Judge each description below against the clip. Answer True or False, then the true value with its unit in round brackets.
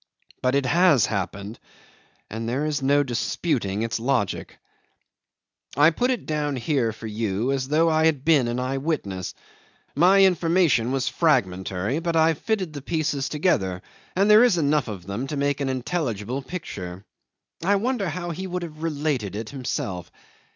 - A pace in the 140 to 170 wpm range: True (160 wpm)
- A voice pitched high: False (140 Hz)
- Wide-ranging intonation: True (6.3 semitones)